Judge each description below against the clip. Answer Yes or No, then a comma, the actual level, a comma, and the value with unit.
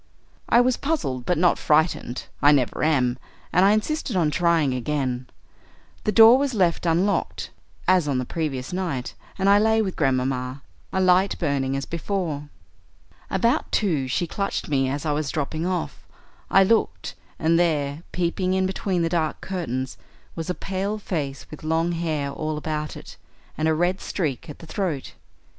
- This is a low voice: No, medium, 165 Hz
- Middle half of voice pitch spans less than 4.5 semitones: No, average, 4.9 semitones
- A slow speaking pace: No, average, 170 wpm